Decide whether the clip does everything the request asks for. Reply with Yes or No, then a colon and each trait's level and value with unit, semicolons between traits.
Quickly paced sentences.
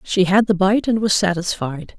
Yes: fast, 210 wpm